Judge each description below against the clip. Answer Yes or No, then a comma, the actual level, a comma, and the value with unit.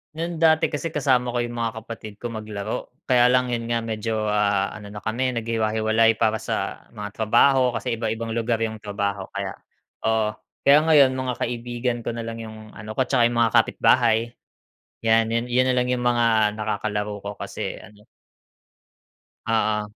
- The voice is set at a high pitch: No, low, 115 Hz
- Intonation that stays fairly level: Yes, narrow, 2.2 semitones